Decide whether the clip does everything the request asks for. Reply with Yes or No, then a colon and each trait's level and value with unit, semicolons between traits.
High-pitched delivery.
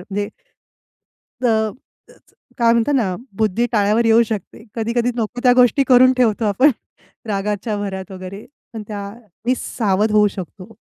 Yes: high, 220 Hz